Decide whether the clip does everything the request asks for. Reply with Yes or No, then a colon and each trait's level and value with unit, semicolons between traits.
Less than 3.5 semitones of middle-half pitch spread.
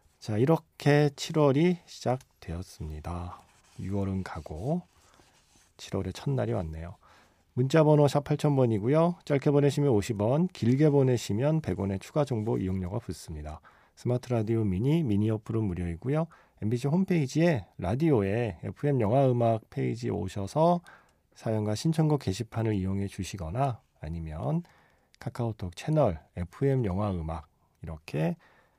No: wide, 7.5 semitones